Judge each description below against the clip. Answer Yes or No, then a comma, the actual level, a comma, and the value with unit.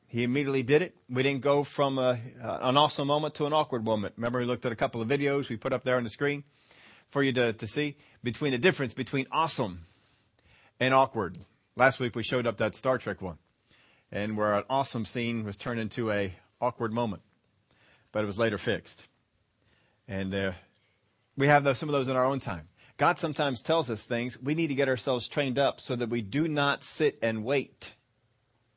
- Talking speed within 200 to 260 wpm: Yes, fast, 205 wpm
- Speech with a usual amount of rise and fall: Yes, average, 3.9 semitones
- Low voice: Yes, low, 125 Hz